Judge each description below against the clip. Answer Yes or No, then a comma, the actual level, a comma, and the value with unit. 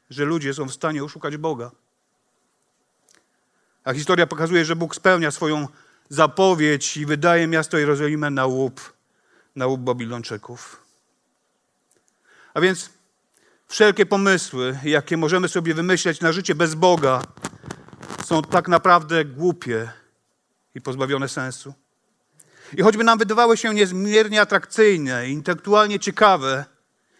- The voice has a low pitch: No, medium, 160 Hz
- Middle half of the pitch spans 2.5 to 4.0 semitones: No, average, 4.8 semitones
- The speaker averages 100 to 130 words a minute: Yes, average, 115 wpm